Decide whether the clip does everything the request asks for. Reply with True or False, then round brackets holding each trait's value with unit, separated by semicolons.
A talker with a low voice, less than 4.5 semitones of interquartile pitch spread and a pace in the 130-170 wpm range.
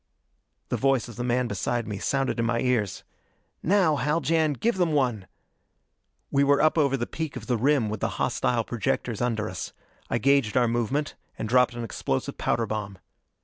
False (125 Hz; 4.0 semitones; 185 wpm)